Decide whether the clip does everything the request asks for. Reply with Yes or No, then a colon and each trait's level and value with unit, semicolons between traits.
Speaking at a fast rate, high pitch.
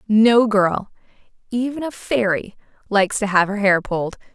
No: average, 150 wpm; high, 210 Hz